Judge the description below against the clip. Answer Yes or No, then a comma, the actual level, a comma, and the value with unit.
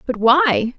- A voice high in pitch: Yes, very high, 260 Hz